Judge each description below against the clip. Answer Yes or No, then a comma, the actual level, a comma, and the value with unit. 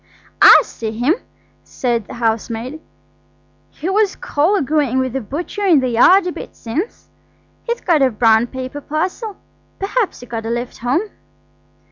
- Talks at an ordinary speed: Yes, average, 150 wpm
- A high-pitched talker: Yes, very high, 270 Hz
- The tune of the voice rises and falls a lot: Yes, wide, 7.2 semitones